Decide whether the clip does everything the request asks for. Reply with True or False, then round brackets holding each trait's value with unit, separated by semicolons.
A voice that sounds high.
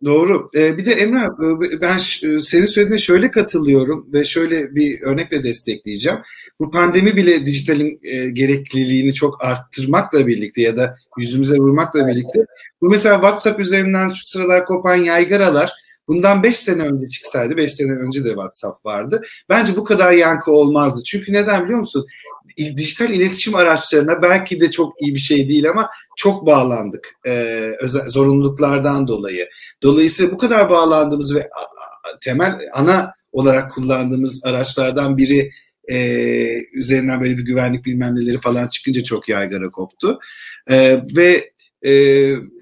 False (145 Hz)